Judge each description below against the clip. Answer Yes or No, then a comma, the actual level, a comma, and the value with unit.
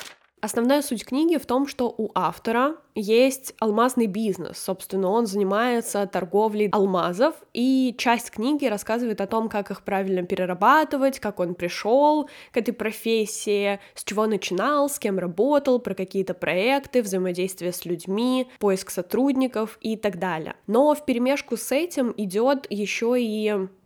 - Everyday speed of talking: Yes, average, 145 wpm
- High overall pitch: Yes, high, 220 Hz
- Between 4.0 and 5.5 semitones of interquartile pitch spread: Yes, average, 4.6 semitones